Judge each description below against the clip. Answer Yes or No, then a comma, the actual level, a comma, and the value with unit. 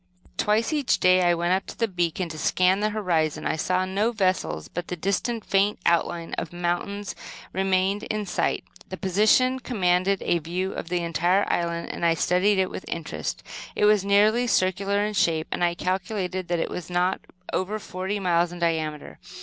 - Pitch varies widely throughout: No, average, 2.7 semitones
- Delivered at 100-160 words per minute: No, average, 185 wpm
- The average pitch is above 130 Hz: Yes, medium, 185 Hz